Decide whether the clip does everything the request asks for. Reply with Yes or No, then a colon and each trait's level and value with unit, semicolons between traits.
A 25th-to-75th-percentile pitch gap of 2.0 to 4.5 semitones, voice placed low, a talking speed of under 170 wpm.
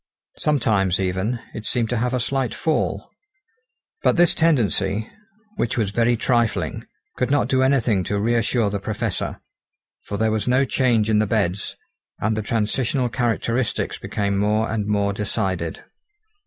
Yes: average, 3.3 semitones; low, 110 Hz; average, 150 wpm